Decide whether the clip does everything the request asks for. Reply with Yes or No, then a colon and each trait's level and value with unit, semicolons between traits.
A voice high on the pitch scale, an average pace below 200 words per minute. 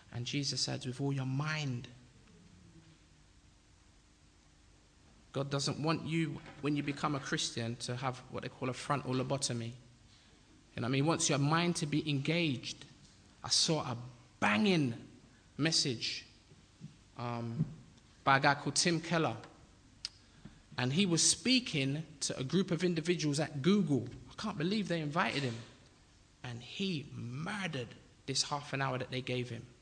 No: low, 135 Hz; average, 150 wpm